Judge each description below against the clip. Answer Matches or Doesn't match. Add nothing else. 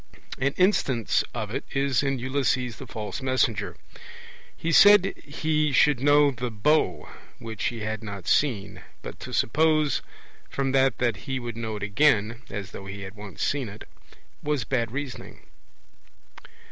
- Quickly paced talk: Doesn't match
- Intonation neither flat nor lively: Matches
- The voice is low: Matches